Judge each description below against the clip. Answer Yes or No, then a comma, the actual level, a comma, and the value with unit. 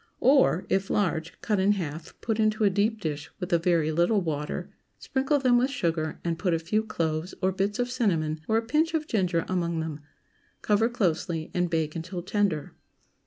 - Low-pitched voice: No, medium, 185 Hz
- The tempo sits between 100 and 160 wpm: No, average, 190 wpm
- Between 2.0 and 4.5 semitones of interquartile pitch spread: No, average, 4.9 semitones